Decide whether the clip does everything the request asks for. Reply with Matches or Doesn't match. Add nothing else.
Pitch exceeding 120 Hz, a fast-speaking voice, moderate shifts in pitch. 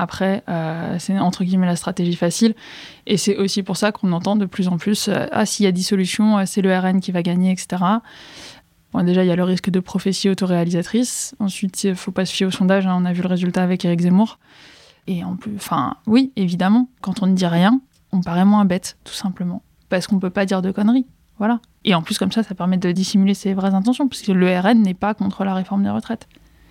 Doesn't match